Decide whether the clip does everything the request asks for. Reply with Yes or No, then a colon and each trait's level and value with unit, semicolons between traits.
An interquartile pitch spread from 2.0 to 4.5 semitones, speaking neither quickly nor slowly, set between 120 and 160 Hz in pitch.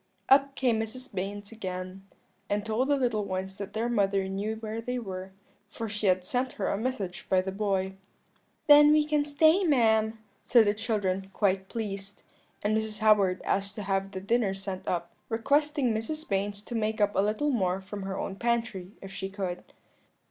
No: average, 3.4 semitones; average, 185 wpm; high, 210 Hz